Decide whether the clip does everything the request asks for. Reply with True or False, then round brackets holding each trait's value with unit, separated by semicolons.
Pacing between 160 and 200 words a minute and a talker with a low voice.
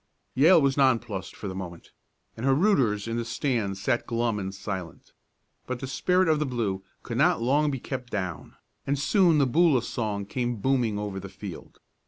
True (190 wpm; 120 Hz)